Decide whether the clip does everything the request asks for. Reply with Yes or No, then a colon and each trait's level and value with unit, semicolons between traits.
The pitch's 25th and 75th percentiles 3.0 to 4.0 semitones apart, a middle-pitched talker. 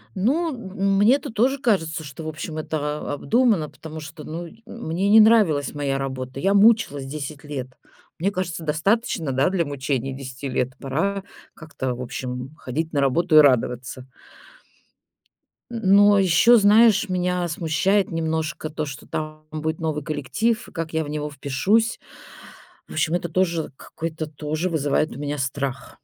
No: average, 5.2 semitones; medium, 160 Hz